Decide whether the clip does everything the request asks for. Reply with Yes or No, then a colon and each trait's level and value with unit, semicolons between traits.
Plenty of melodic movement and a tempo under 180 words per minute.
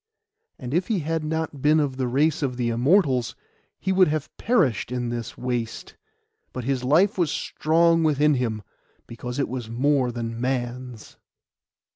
No: average, 4.3 semitones; average, 160 wpm